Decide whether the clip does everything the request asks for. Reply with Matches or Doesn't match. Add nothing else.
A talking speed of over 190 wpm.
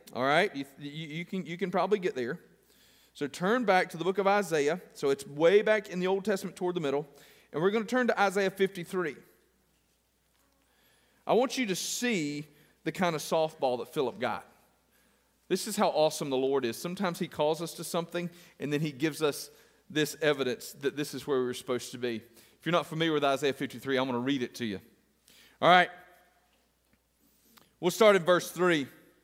Matches